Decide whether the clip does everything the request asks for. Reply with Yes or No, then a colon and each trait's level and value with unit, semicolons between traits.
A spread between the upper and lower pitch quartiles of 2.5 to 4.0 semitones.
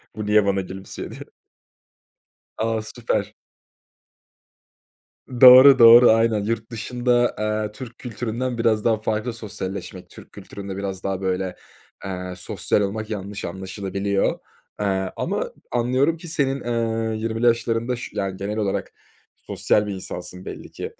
Yes: average, 3.1 semitones